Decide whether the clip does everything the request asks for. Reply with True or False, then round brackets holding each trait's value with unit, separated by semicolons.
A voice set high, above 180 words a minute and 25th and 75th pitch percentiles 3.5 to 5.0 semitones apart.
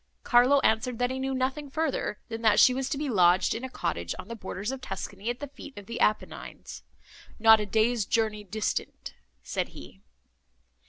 True (230 Hz; 190 wpm; 3.8 semitones)